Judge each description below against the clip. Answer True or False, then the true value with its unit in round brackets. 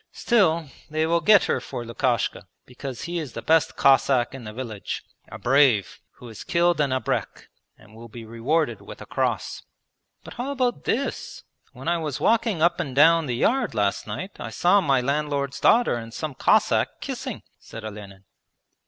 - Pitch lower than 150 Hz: True (140 Hz)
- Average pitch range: False (6.2 semitones)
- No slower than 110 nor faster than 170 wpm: False (180 wpm)